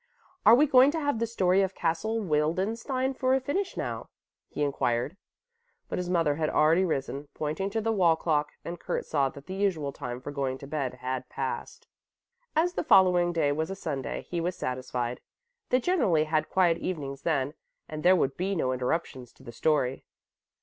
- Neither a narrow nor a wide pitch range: No, wide, 5.7 semitones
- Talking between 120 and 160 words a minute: No, average, 190 wpm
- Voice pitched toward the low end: No, medium, 165 Hz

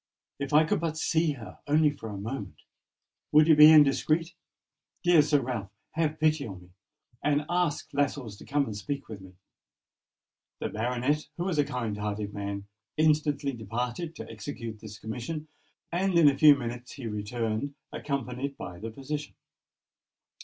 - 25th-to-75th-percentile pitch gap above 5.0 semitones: Yes, wide, 5.4 semitones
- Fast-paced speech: No, average, 160 wpm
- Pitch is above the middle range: No, medium, 140 Hz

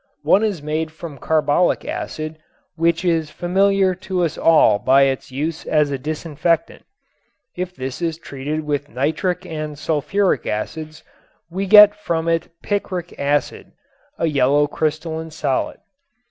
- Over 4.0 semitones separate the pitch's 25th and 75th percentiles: No, average, 3.1 semitones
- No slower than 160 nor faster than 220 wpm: No, slow, 135 wpm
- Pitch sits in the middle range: Yes, medium, 160 Hz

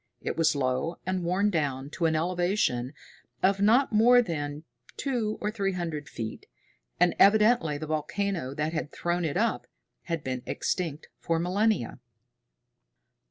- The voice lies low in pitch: No, medium, 170 Hz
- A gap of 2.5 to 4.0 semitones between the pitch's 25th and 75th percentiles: No, average, 5.0 semitones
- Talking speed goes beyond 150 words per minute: No, average, 145 wpm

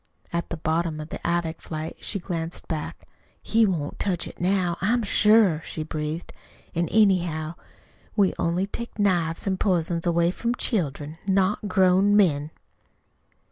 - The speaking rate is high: No, average, 145 wpm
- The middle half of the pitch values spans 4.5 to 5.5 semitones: No, average, 3.4 semitones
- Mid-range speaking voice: Yes, medium, 175 Hz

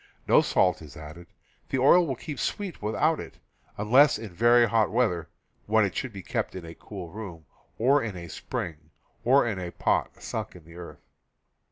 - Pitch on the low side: Yes, low, 105 Hz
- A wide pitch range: Yes, wide, 5.8 semitones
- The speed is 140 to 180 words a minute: No, average, 190 wpm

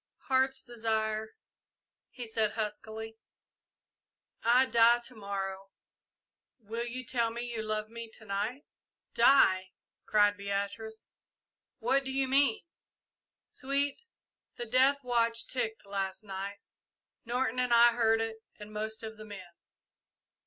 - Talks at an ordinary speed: No, slow, 125 wpm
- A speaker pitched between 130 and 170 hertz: No, high, 225 Hz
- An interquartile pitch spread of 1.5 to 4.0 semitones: Yes, narrow, 2.4 semitones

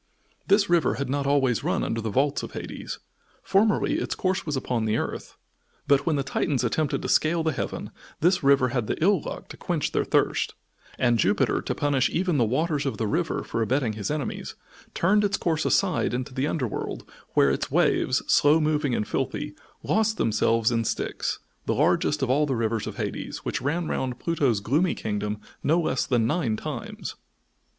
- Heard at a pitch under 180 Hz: Yes, medium, 140 Hz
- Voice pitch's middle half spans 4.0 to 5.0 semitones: No, wide, 5.4 semitones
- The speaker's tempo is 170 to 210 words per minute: Yes, average, 190 wpm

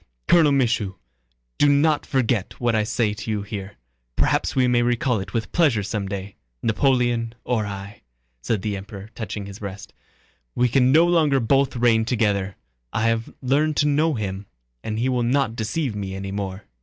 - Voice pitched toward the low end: Yes, low, 115 Hz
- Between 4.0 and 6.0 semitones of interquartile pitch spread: Yes, average, 4.3 semitones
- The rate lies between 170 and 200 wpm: Yes, average, 175 wpm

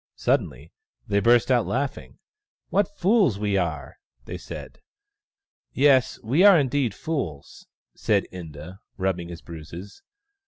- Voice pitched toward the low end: Yes, low, 105 Hz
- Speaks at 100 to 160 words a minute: Yes, average, 140 wpm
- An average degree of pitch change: No, wide, 8.5 semitones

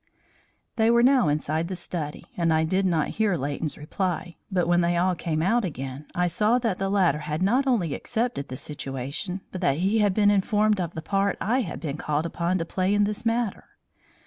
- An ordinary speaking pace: No, fast, 210 wpm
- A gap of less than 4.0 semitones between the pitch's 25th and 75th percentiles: No, average, 4.6 semitones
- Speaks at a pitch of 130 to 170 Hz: No, medium, 180 Hz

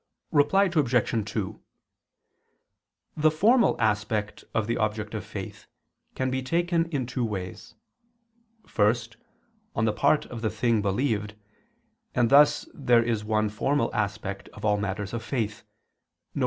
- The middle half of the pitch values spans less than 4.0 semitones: No, average, 4.3 semitones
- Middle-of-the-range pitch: No, low, 115 Hz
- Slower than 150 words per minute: Yes, average, 140 wpm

